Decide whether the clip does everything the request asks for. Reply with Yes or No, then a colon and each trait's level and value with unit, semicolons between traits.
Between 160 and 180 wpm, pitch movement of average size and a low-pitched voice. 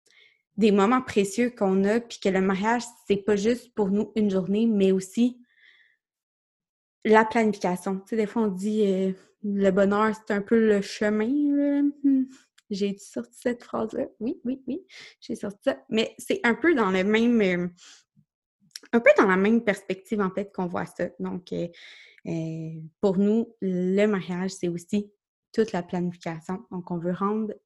No: average, 175 wpm; average, 3.5 semitones; high, 210 Hz